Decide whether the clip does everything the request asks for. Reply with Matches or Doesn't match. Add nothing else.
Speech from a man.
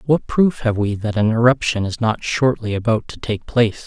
Matches